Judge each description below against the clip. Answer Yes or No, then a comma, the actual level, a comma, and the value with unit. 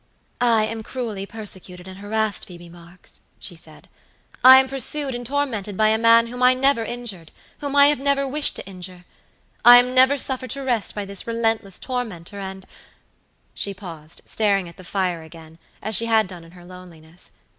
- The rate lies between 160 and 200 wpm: Yes, average, 185 wpm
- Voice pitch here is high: Yes, high, 215 Hz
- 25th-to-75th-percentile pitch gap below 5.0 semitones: No, average, 5.3 semitones